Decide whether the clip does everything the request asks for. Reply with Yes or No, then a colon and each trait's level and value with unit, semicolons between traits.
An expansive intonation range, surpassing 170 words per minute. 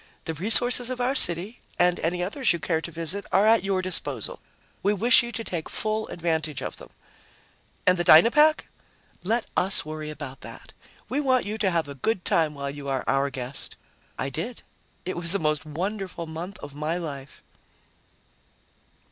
Yes: wide, 5.8 semitones; average, 180 wpm